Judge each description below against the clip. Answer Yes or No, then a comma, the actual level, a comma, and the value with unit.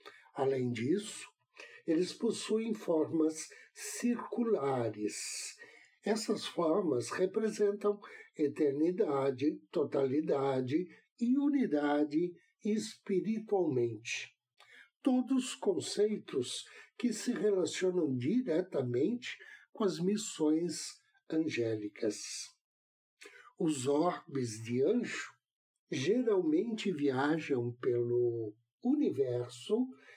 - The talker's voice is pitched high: No, medium, 170 Hz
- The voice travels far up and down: Yes, wide, 8.4 semitones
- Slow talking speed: Yes, slow, 65 wpm